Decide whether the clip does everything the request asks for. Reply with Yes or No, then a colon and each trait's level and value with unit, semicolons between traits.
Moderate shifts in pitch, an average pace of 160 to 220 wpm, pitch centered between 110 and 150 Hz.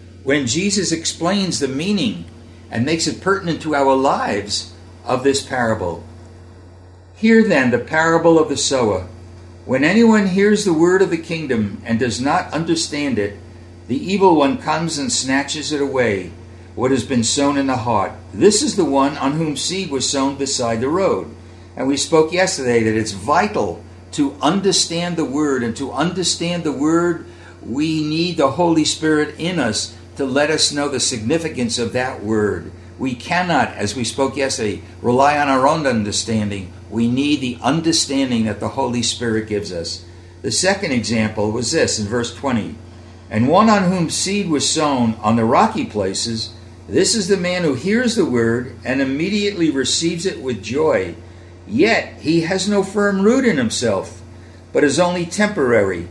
No: wide, 7.5 semitones; average, 170 wpm; low, 135 Hz